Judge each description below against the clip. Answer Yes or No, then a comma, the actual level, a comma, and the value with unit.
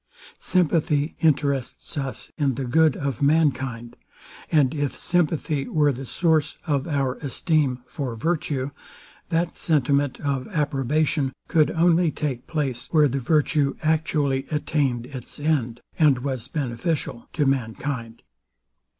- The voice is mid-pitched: Yes, medium, 145 Hz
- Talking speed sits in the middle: No, slow, 125 wpm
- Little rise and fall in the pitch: No, average, 3.0 semitones